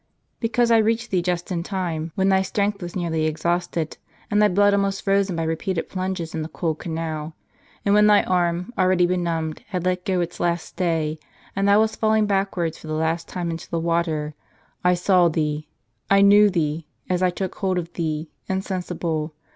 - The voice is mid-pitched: Yes, medium, 180 Hz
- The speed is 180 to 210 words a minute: Yes, average, 195 wpm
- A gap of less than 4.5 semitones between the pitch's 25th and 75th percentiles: Yes, average, 3.1 semitones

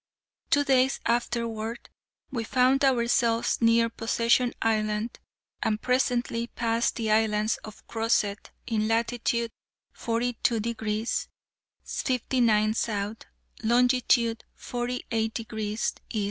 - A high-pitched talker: Yes, high, 230 Hz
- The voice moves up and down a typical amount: No, narrow, 1.7 semitones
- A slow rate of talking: Yes, slow, 95 wpm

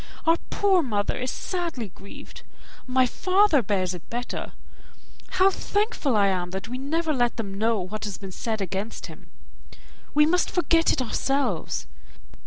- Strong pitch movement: Yes, wide, 8.3 semitones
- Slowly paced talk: No, average, 155 wpm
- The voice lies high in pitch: Yes, high, 245 Hz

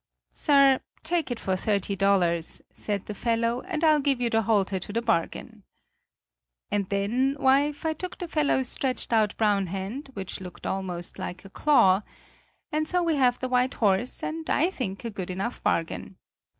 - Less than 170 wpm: No, average, 175 wpm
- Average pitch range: No, wide, 6.2 semitones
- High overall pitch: Yes, high, 230 Hz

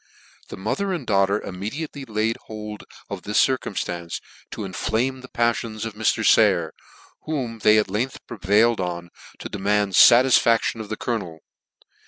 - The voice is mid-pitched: No, low, 110 Hz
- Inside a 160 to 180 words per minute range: No, average, 145 wpm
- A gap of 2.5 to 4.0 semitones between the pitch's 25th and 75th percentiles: Yes, average, 3.1 semitones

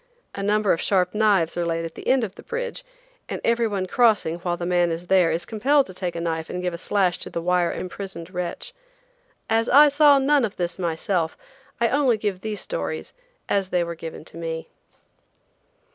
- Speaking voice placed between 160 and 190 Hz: Yes, medium, 185 Hz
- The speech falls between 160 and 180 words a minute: No, fast, 205 wpm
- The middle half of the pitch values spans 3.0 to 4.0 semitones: No, average, 4.6 semitones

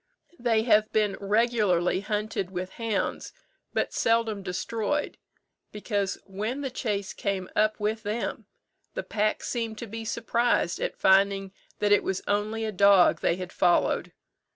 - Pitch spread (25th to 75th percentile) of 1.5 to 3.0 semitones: Yes, narrow, 2.4 semitones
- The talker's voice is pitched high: Yes, high, 210 Hz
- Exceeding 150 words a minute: No, average, 145 wpm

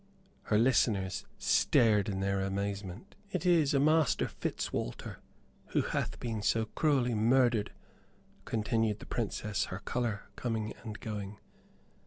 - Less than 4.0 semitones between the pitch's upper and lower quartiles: Yes, average, 3.4 semitones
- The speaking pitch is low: Yes, low, 110 Hz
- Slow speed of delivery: Yes, slow, 125 wpm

